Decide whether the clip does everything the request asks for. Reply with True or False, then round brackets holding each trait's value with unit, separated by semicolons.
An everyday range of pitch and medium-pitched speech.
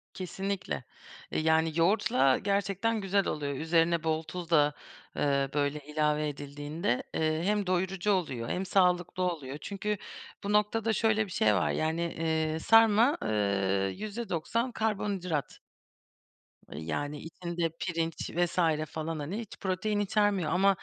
True (4.8 semitones; 170 Hz)